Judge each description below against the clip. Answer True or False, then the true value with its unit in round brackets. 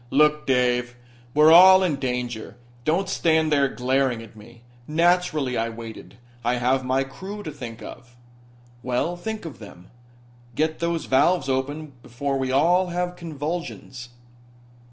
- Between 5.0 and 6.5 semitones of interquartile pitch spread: True (5.3 semitones)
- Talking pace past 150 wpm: False (140 wpm)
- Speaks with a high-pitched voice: False (140 Hz)